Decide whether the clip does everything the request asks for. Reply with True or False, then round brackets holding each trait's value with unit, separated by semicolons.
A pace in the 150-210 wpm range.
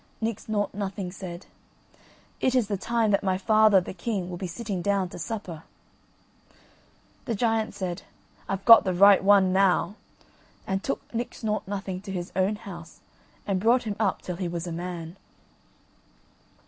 True (165 wpm)